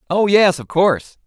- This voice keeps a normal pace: Yes, average, 190 wpm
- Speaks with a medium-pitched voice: Yes, medium, 175 Hz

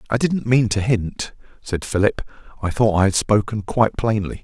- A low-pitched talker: Yes, low, 110 Hz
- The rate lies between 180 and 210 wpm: Yes, fast, 205 wpm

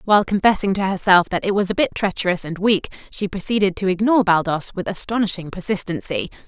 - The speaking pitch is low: No, high, 195 Hz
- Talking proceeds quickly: No, average, 185 wpm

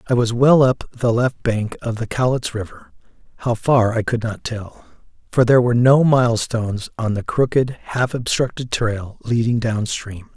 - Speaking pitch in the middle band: No, low, 115 Hz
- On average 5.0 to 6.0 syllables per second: No, 4.7 syllables/s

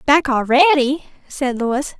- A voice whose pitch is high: Yes, very high, 275 Hz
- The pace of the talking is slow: Yes, slow, 120 wpm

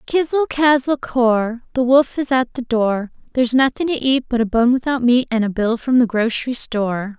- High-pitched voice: Yes, high, 245 Hz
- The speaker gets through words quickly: Yes, fast, 210 wpm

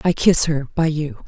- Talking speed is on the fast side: Yes, fast, 235 wpm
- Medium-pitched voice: Yes, medium, 155 Hz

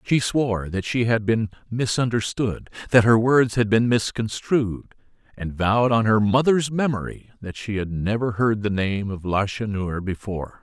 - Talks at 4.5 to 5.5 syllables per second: Yes, 4.6 syllables/s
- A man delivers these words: Yes, male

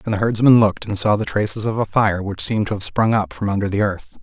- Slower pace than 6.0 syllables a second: No, 6.4 syllables/s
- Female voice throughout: No, male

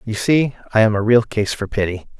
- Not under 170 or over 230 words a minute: No, fast, 245 wpm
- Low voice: Yes, low, 110 Hz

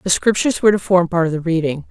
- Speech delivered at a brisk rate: Yes, fast, 285 wpm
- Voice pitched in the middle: Yes, medium, 175 Hz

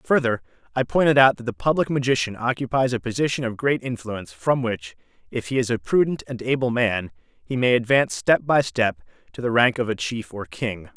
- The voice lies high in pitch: No, low, 120 Hz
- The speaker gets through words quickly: Yes, fast, 210 wpm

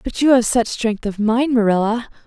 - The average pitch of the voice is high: Yes, high, 230 Hz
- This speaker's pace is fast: Yes, fast, 210 wpm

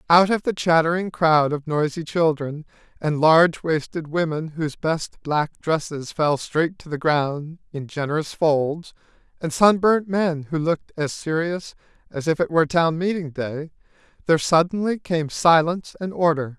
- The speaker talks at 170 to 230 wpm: No, average, 160 wpm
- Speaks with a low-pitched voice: No, medium, 160 Hz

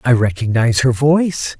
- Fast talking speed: No, average, 150 wpm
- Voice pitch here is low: Yes, low, 130 Hz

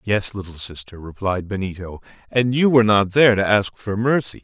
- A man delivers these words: Yes, male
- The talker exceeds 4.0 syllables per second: Yes, 5.4 syllables/s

